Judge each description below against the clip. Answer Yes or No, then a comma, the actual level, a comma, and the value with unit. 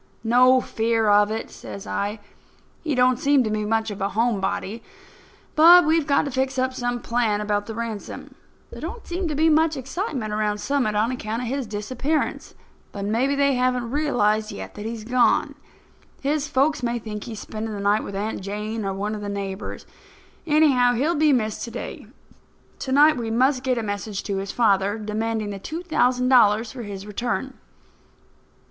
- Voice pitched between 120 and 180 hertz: No, high, 230 Hz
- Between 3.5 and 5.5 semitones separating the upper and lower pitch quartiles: Yes, average, 4.0 semitones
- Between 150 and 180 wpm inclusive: No, average, 190 wpm